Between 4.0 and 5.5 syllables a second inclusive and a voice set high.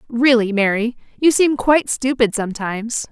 Yes: 5.2 syllables/s; high, 240 Hz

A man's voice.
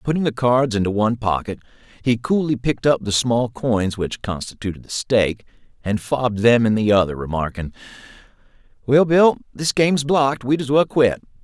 Yes: male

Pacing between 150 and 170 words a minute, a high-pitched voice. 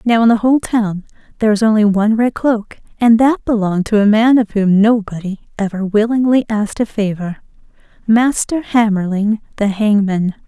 Yes: average, 160 wpm; high, 215 Hz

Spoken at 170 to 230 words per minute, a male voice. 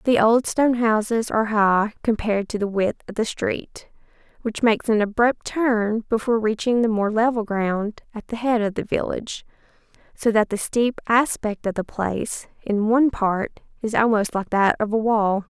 No: average, 185 wpm; female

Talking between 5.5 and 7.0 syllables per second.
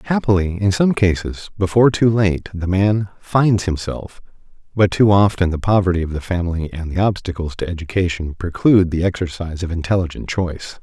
Yes: 5.6 syllables/s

